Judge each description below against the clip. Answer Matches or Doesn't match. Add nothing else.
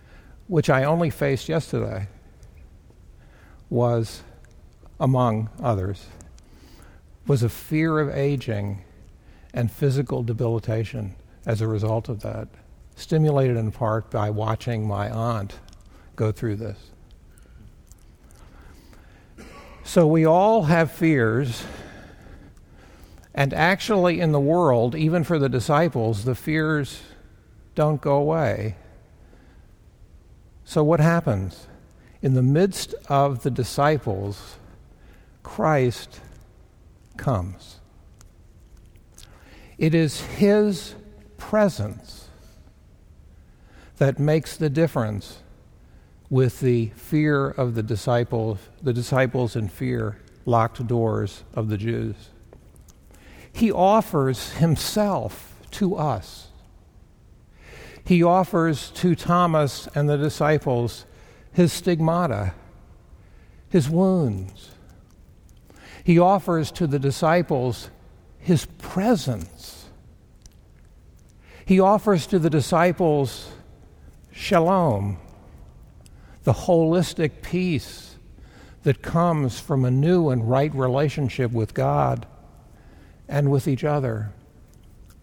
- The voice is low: Matches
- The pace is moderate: Doesn't match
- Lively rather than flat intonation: Matches